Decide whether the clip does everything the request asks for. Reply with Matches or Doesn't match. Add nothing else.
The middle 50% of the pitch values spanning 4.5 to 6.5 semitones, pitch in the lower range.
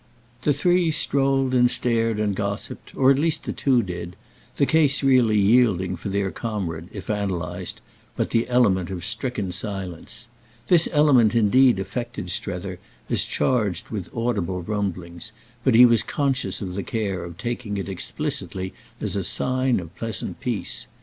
Matches